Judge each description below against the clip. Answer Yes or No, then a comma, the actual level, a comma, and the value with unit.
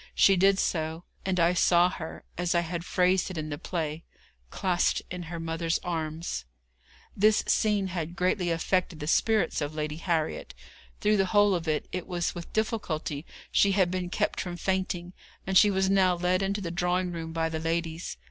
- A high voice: No, medium, 175 Hz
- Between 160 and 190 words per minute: Yes, average, 185 wpm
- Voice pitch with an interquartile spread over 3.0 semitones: No, narrow, 2.5 semitones